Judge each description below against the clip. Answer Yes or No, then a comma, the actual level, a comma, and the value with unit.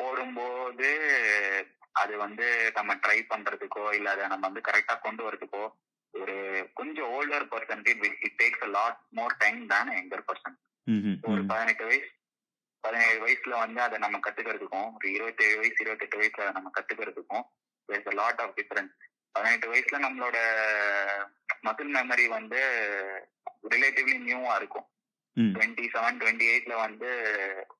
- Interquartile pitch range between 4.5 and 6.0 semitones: No, average, 3.0 semitones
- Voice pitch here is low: Yes, low, 110 Hz